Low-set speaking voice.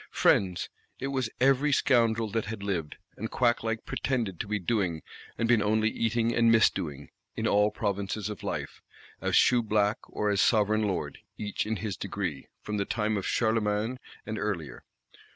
Yes: low, 105 Hz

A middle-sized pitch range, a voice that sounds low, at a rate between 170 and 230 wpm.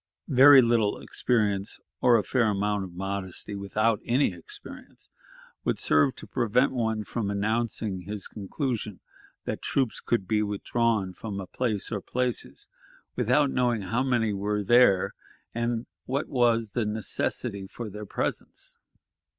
No: average, 3.2 semitones; low, 110 Hz; average, 140 wpm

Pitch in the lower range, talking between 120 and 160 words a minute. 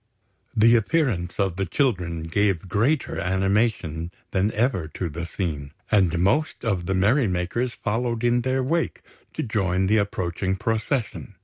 Yes: low, 100 Hz; average, 145 wpm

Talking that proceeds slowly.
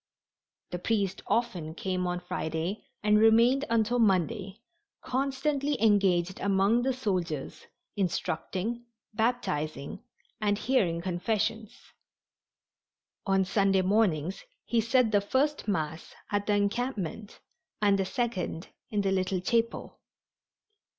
Yes: slow, 110 wpm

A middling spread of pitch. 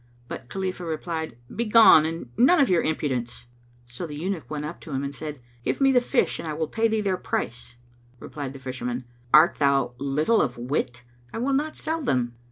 No: wide, 7.1 semitones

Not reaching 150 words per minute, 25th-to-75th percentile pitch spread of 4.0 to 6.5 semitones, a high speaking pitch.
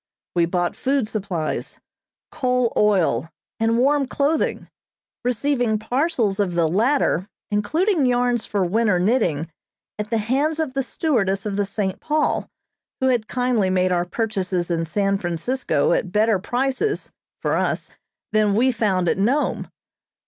Yes: average, 140 wpm; average, 5.2 semitones; high, 215 Hz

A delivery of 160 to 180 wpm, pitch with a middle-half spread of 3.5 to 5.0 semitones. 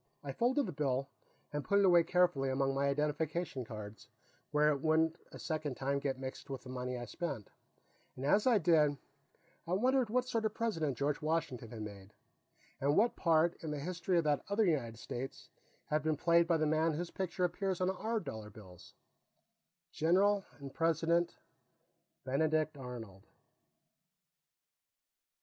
Yes: average, 165 wpm; average, 4.6 semitones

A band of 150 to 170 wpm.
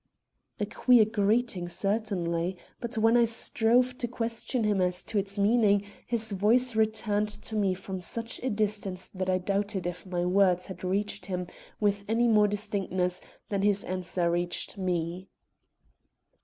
Yes: average, 155 wpm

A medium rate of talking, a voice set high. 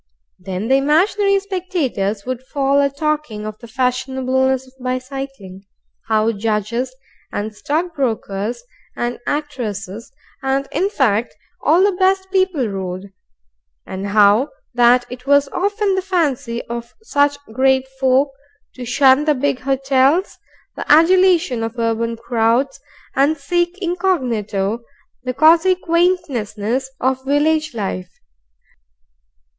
No: slow, 120 wpm; very high, 265 Hz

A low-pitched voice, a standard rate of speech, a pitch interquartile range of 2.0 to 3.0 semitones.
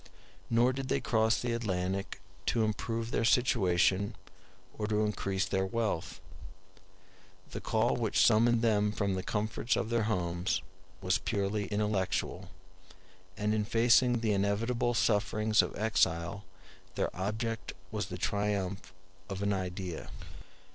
No: low, 105 Hz; slow, 130 wpm; average, 2.7 semitones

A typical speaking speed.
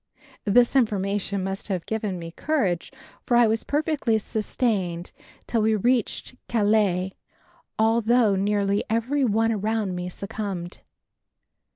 No: slow, 115 wpm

